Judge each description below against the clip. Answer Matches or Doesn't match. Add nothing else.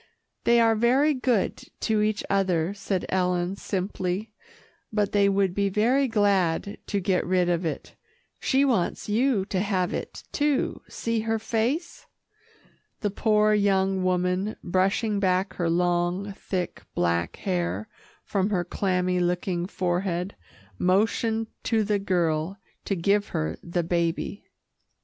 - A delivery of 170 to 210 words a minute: Doesn't match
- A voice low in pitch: Doesn't match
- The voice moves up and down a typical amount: Matches